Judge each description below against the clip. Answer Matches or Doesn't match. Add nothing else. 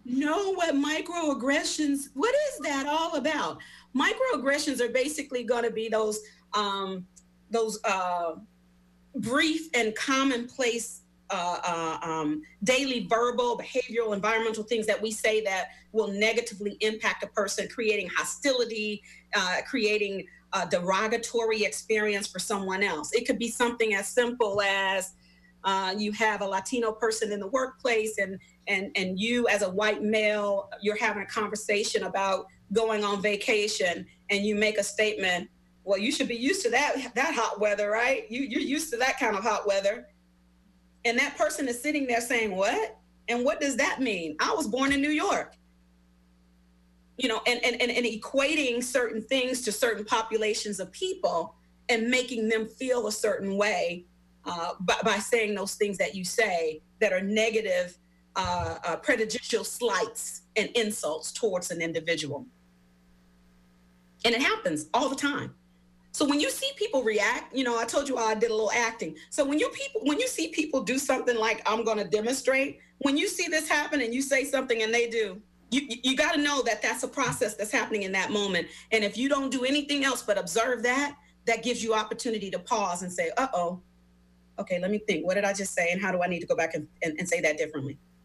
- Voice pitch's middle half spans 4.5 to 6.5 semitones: Matches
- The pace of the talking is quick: Doesn't match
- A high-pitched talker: Matches